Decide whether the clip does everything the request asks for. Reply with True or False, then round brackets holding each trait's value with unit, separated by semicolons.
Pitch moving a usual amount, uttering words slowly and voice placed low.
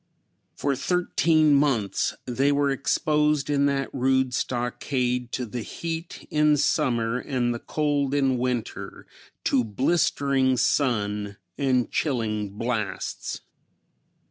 True (3.0 semitones; 110 wpm; 130 Hz)